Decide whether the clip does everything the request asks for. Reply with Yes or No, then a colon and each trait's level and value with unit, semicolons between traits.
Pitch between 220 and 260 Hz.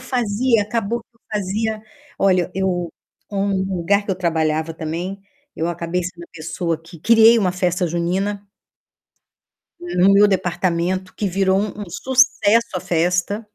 No: high, 190 Hz